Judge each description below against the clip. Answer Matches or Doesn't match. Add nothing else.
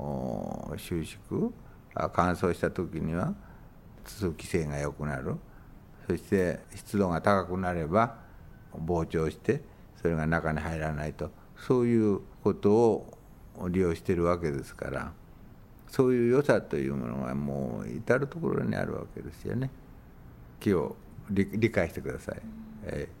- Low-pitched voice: Matches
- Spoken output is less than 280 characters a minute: Matches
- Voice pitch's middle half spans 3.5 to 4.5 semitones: Doesn't match